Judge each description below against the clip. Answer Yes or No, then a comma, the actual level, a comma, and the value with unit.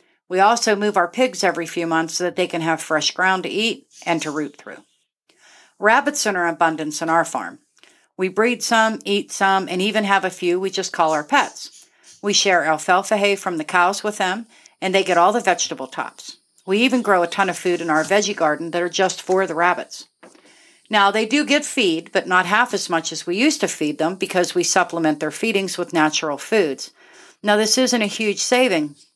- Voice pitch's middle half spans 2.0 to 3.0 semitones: No, average, 3.7 semitones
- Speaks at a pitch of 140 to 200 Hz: Yes, medium, 185 Hz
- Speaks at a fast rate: Yes, fast, 220 wpm